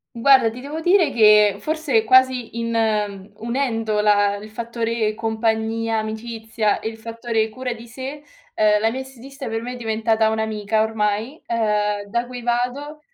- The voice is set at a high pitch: Yes, high, 225 Hz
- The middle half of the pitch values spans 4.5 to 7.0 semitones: No, narrow, 2.4 semitones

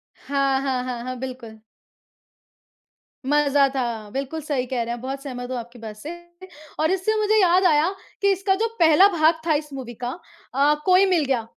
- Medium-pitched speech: No, very high, 275 Hz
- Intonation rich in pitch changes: No, average, 4.5 semitones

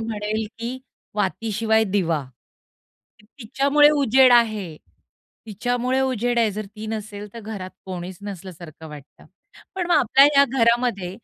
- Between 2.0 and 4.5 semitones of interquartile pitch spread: Yes, average, 3.9 semitones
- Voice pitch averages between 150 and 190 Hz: No, high, 220 Hz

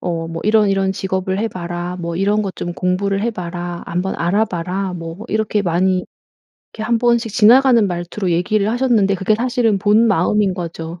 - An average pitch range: Yes, average, 3.5 semitones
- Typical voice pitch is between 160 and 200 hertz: Yes, high, 195 Hz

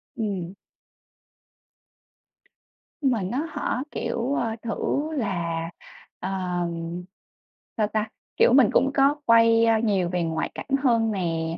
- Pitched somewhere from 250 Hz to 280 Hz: No, high, 220 Hz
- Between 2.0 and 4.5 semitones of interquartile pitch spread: No, average, 5.0 semitones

